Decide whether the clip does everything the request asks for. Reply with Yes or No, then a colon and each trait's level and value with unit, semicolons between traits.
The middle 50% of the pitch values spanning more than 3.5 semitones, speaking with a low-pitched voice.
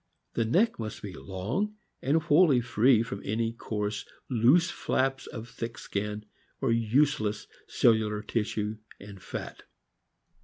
Yes: average, 4.0 semitones; low, 115 Hz